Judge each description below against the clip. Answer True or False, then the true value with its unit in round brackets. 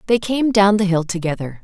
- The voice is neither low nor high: False (195 Hz)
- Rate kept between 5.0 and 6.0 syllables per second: True (5.5 syllables/s)